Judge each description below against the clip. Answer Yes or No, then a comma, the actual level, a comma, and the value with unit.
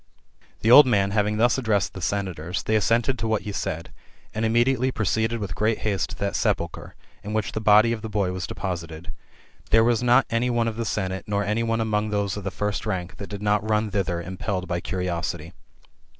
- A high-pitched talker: No, low, 105 Hz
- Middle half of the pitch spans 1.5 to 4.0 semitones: Yes, average, 3.0 semitones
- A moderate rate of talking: No, fast, 210 wpm